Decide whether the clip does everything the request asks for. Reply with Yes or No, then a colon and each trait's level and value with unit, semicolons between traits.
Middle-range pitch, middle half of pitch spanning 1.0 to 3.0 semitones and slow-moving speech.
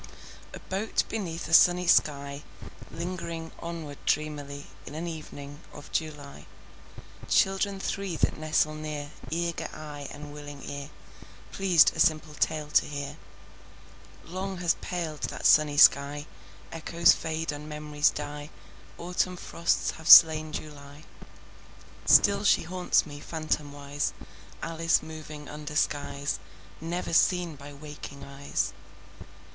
Yes: medium, 155 Hz; narrow, 2.5 semitones; slow, 120 wpm